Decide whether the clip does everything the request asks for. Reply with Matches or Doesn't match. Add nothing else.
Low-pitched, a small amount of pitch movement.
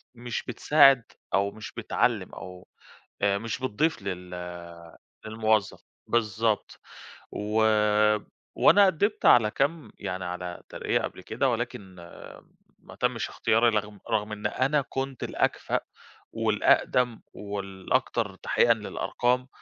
Doesn't match